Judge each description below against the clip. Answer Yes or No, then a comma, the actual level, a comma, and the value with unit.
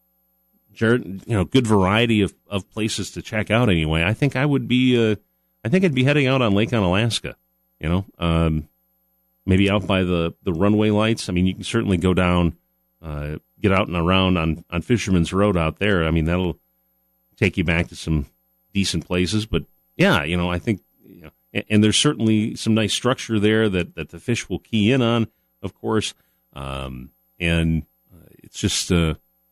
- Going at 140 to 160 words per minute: No, average, 195 wpm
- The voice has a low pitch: Yes, very low, 90 Hz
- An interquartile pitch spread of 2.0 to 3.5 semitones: No, average, 5.1 semitones